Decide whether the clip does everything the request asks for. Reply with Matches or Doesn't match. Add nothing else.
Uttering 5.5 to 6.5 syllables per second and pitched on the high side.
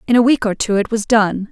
Matches